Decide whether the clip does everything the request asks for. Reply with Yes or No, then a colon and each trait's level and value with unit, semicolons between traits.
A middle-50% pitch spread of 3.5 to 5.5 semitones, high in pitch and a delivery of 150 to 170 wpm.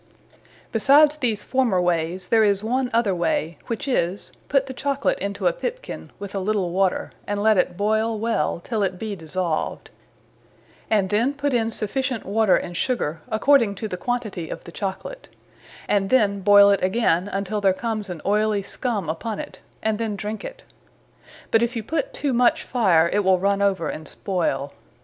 No: average, 3.9 semitones; high, 210 Hz; average, 180 wpm